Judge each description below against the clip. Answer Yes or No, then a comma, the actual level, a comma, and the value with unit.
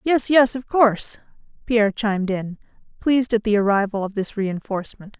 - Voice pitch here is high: Yes, high, 220 Hz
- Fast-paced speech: No, average, 160 wpm